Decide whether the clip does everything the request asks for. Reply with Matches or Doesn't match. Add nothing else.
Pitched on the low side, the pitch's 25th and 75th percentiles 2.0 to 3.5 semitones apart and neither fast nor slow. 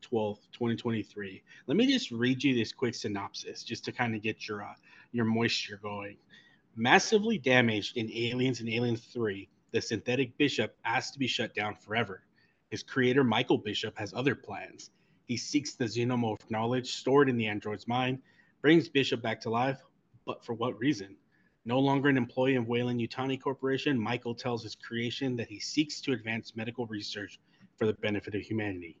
Matches